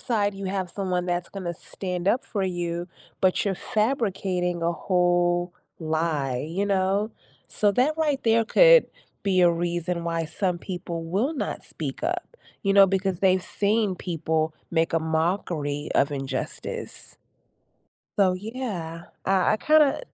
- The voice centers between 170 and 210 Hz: Yes, medium, 185 Hz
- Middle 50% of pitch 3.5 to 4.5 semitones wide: No, average, 3.1 semitones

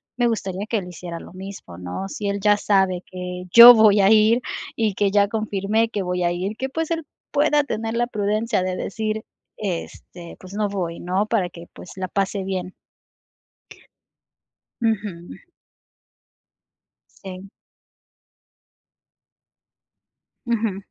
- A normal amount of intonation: Yes, average, 3.0 semitones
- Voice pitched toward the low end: No, high, 200 Hz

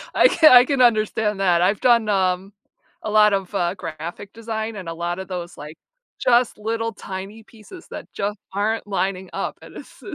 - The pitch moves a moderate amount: Yes, average, 3.2 semitones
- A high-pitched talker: Yes, high, 205 Hz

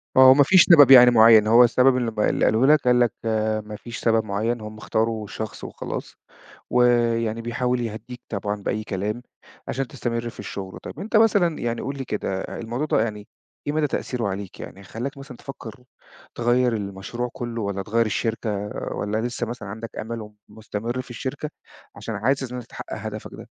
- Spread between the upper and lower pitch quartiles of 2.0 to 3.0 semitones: Yes, narrow, 2.6 semitones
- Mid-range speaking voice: No, low, 115 Hz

